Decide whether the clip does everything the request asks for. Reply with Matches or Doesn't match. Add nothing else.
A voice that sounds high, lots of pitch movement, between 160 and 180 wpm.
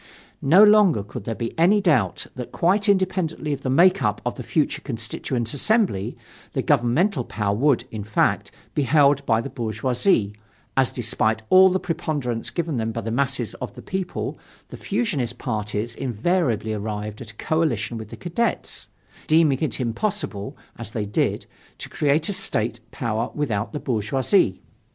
Doesn't match